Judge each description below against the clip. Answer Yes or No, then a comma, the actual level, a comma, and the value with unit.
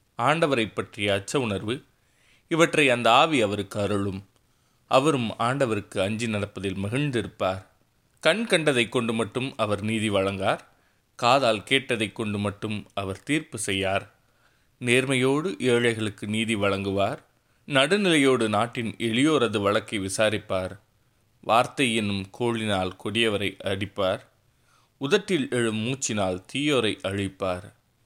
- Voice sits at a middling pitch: No, low, 110 Hz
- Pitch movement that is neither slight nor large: Yes, average, 3.9 semitones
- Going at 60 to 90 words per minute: No, average, 100 wpm